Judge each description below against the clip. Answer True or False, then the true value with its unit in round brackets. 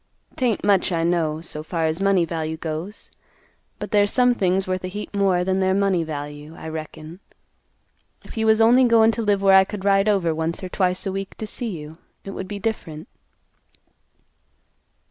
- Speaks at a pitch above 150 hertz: True (190 Hz)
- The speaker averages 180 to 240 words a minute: True (190 wpm)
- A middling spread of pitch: True (4.0 semitones)